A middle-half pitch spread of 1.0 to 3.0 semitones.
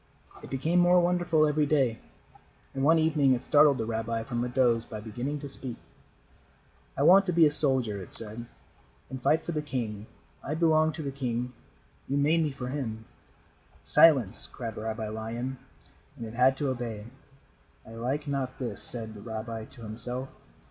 No: average, 4.5 semitones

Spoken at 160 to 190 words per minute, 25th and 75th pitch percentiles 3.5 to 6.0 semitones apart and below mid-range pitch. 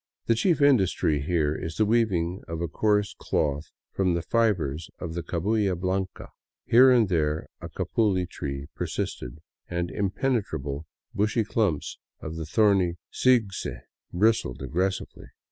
No: slow, 135 wpm; average, 5.1 semitones; very low, 90 Hz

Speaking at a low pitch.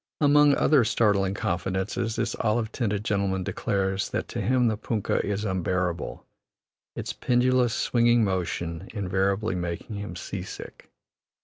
Yes: low, 100 Hz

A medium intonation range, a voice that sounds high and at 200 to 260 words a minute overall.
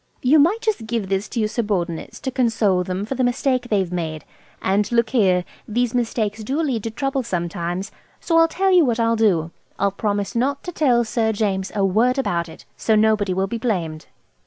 Yes: average, 4.6 semitones; high, 220 Hz; fast, 205 wpm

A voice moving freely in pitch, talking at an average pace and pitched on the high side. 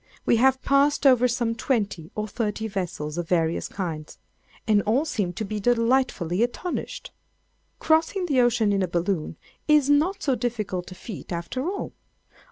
Yes: wide, 6.2 semitones; average, 160 wpm; high, 225 Hz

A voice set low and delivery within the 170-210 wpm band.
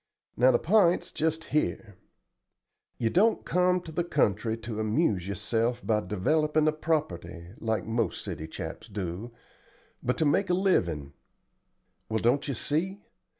No: low, 125 Hz; average, 145 wpm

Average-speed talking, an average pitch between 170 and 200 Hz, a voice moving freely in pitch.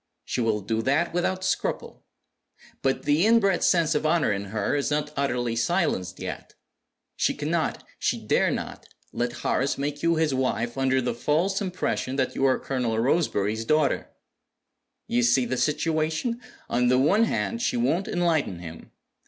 No: average, 160 wpm; medium, 140 Hz; wide, 5.7 semitones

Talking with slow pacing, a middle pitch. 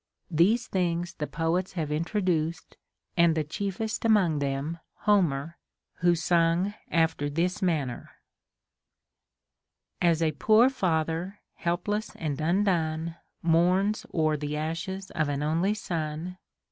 Yes: slow, 120 wpm; medium, 170 Hz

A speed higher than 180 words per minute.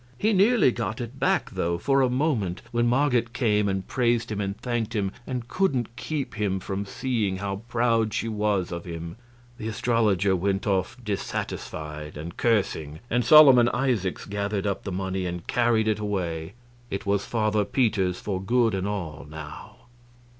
No: average, 170 wpm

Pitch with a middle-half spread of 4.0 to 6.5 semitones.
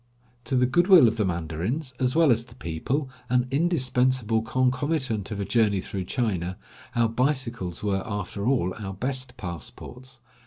Yes: average, 4.6 semitones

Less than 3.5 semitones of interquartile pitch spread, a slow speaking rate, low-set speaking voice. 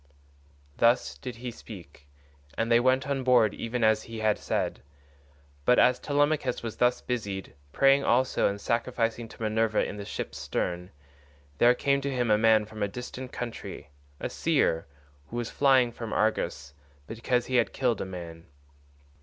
No: average, 2.9 semitones; average, 165 wpm; low, 115 Hz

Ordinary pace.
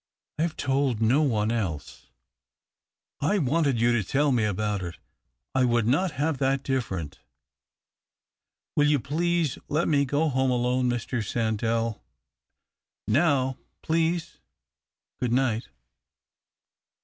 No: slow, 125 wpm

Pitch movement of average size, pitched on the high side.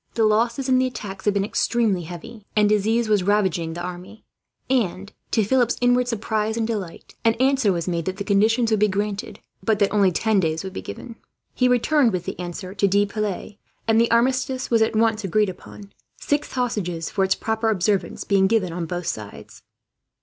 Yes: average, 3.3 semitones; high, 210 Hz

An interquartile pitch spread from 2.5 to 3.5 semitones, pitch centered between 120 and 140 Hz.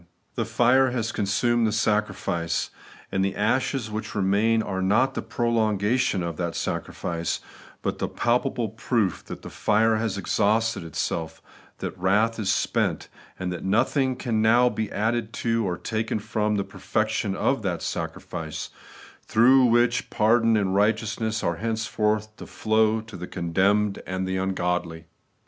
No: average, 3.1 semitones; low, 110 Hz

